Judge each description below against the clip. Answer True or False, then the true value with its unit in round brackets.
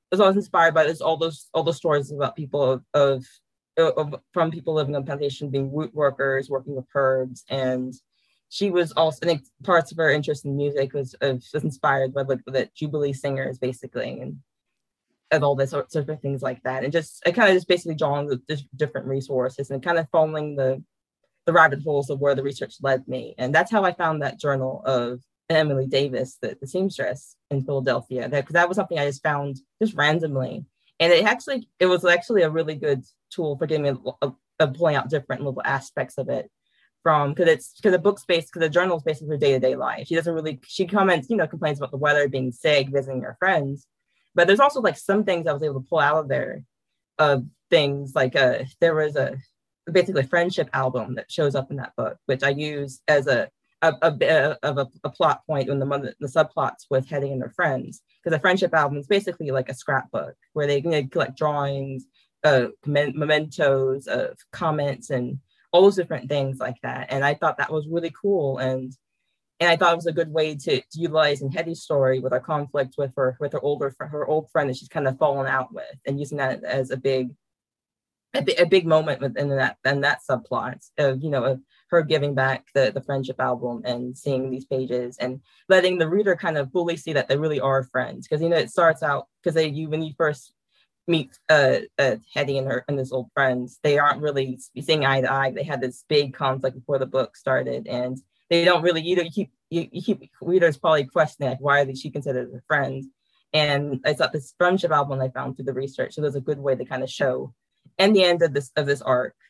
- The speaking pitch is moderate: True (145 Hz)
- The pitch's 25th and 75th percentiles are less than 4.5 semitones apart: True (3.4 semitones)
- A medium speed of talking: False (225 wpm)